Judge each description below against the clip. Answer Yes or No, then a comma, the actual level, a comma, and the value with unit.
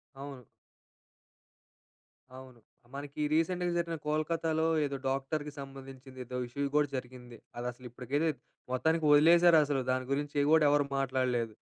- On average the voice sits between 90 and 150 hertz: Yes, medium, 140 Hz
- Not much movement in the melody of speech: No, average, 3.3 semitones